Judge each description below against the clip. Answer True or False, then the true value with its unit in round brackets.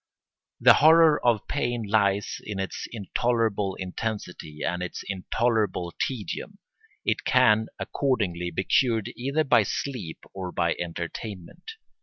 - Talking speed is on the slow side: True (120 wpm)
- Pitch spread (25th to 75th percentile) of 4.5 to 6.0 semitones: True (4.9 semitones)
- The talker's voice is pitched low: True (105 Hz)